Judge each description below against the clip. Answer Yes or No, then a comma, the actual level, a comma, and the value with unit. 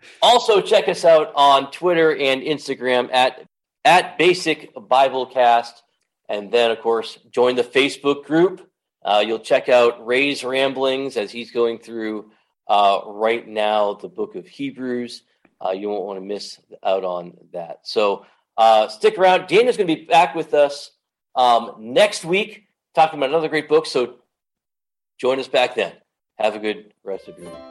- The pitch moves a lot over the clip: Yes, wide, 5.8 semitones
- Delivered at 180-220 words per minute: No, average, 165 wpm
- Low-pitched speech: Yes, low, 130 Hz